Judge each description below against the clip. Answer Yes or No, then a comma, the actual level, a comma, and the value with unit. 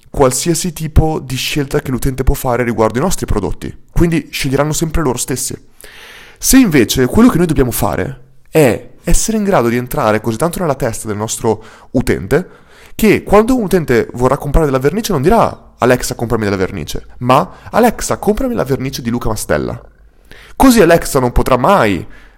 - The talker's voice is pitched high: No, low, 135 Hz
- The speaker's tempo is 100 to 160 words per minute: No, fast, 170 wpm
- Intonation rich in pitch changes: Yes, wide, 6.1 semitones